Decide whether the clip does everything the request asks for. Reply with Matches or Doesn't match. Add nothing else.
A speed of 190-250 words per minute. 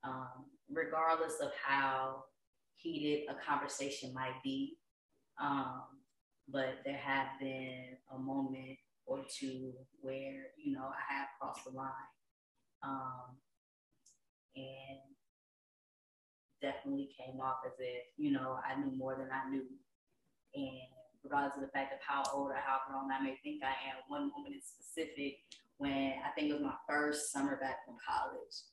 Doesn't match